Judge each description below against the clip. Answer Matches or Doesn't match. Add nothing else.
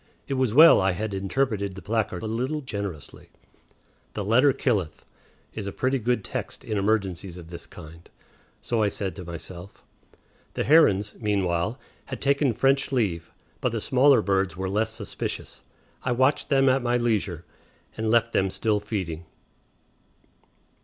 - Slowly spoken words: Doesn't match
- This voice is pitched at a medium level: Doesn't match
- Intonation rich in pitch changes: Doesn't match